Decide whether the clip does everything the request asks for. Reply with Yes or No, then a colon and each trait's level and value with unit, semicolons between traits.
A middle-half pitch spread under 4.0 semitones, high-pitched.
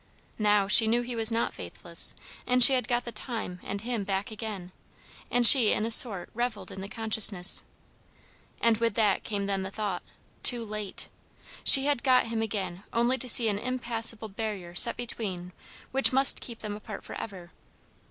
Yes: average, 3.0 semitones; high, 220 Hz